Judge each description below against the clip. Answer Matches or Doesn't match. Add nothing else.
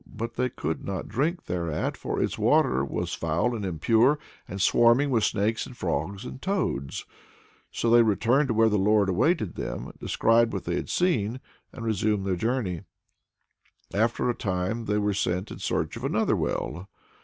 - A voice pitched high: Doesn't match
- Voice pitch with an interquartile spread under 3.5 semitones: Doesn't match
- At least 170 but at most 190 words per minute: Matches